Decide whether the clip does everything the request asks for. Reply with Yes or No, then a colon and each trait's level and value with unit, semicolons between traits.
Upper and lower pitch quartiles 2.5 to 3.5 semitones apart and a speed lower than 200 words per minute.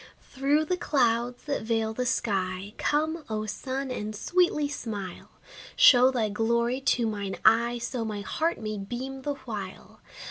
No: average, 4.0 semitones; average, 150 wpm